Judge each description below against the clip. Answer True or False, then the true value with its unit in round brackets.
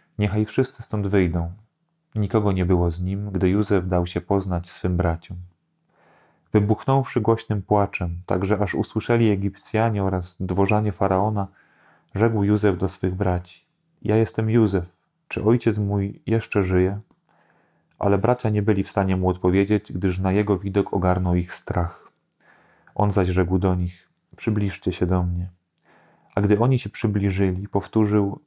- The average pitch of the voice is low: True (100 Hz)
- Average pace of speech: True (145 wpm)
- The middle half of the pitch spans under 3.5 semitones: True (2.8 semitones)